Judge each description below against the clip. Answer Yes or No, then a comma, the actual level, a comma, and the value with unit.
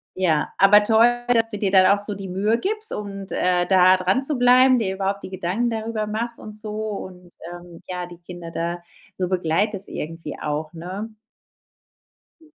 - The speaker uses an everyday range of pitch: Yes, average, 3.7 semitones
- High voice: Yes, high, 195 Hz